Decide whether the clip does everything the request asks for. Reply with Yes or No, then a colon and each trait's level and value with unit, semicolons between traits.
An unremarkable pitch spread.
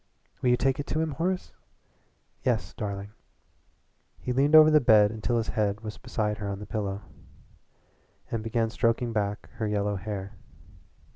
Yes: average, 3.4 semitones